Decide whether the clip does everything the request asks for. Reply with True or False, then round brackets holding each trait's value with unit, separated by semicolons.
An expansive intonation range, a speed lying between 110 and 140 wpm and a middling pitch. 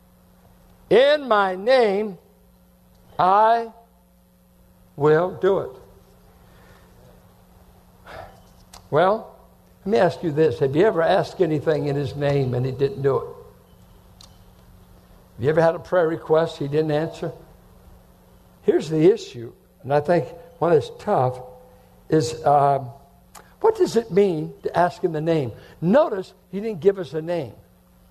True (6.4 semitones; 135 wpm; 160 Hz)